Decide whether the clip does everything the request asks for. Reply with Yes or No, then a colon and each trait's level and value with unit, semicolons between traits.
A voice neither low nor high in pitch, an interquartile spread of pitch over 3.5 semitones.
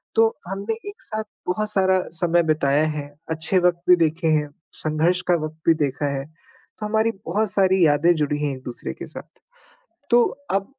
Yes: medium, 175 Hz; average, 4.3 semitones